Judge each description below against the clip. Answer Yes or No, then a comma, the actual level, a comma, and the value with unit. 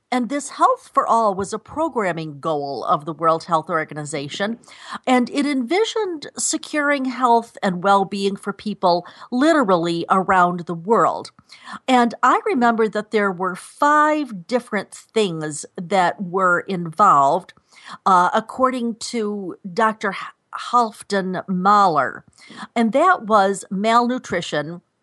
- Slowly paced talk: Yes, slow, 120 wpm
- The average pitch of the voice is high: Yes, high, 205 Hz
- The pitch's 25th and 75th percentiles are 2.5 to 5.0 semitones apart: No, wide, 5.6 semitones